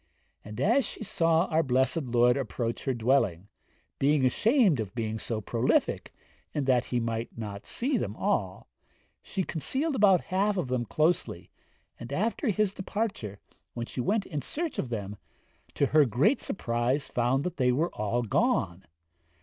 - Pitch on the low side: Yes, low, 130 Hz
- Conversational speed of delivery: Yes, average, 160 wpm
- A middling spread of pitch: No, wide, 8.1 semitones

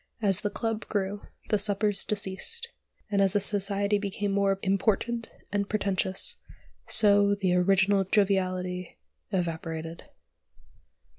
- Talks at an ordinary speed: No, slow, 105 wpm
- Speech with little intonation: Yes, narrow, 1.6 semitones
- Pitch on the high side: Yes, high, 200 Hz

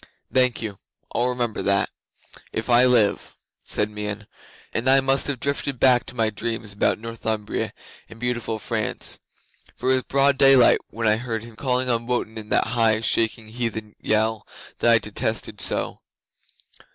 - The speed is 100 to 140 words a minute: No, average, 165 wpm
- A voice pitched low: Yes, low, 115 Hz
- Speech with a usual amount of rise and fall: No, narrow, 2.3 semitones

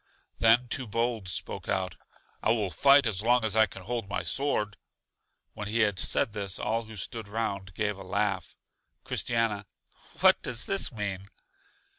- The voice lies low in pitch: Yes, low, 110 Hz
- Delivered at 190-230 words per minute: No, average, 165 wpm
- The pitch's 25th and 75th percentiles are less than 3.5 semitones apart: Yes, average, 2.8 semitones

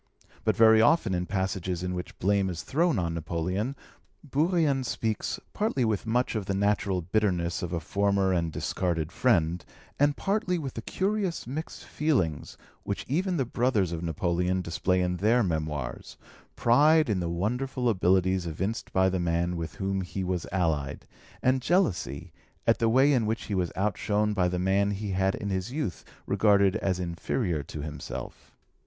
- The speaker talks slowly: No, average, 165 wpm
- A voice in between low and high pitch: No, very low, 95 Hz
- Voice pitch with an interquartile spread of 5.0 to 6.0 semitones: Yes, average, 5.3 semitones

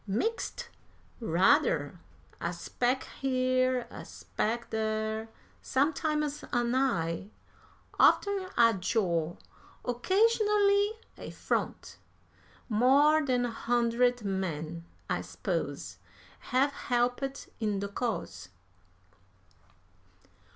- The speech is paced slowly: Yes, slow, 85 wpm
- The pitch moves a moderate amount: Yes, average, 4.9 semitones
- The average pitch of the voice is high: Yes, high, 245 Hz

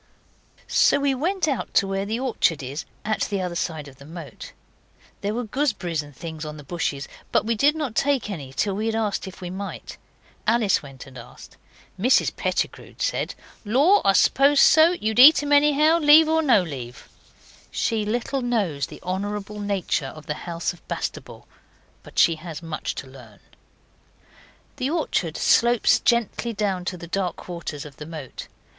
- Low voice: No, high, 200 Hz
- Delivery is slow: No, average, 175 wpm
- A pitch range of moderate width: No, wide, 7.5 semitones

